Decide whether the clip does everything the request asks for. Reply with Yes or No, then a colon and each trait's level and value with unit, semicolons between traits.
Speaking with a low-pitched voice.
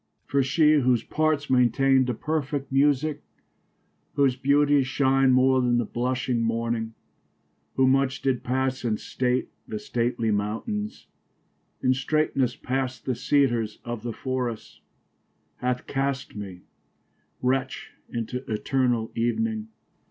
Yes: low, 130 Hz